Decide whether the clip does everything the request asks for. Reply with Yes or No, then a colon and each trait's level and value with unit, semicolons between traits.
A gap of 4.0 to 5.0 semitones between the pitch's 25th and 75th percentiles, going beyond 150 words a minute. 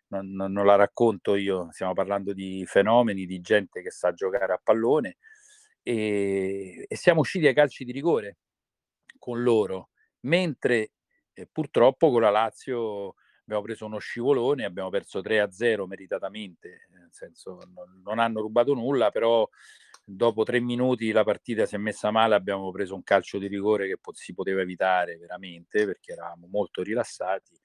Yes: average, 4.5 semitones; average, 160 wpm